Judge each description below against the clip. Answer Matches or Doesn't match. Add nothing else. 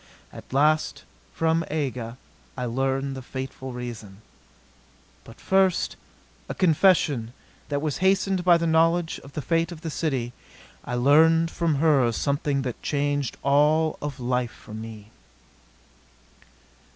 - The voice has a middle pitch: Matches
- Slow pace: Matches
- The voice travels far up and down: Doesn't match